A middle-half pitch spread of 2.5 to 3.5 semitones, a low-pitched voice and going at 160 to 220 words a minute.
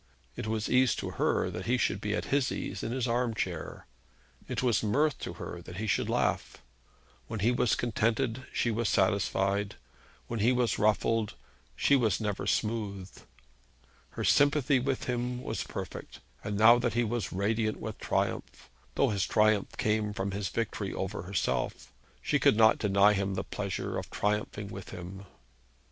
Yes: average, 3.2 semitones; low, 110 Hz; average, 170 wpm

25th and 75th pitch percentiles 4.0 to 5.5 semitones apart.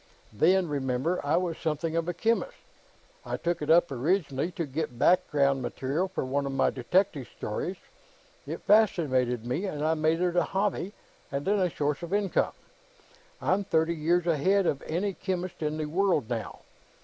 Yes: average, 4.5 semitones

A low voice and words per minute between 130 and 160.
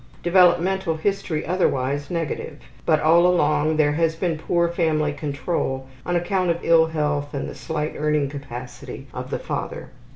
No: medium, 160 Hz; average, 155 wpm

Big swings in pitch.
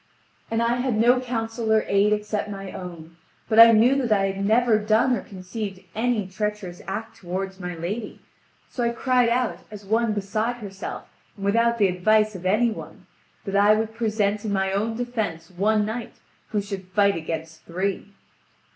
No: average, 2.8 semitones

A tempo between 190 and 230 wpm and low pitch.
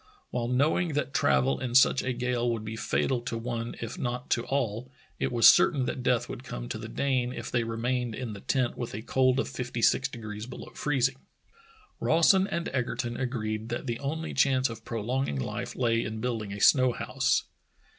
Yes: average, 195 wpm; low, 120 Hz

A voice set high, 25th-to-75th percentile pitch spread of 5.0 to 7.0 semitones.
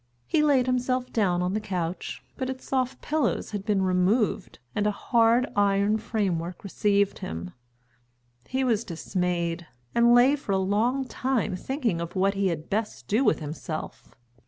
Yes: high, 205 Hz; average, 5.3 semitones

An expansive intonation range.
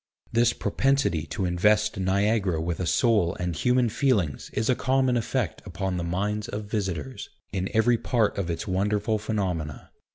No: average, 4.2 semitones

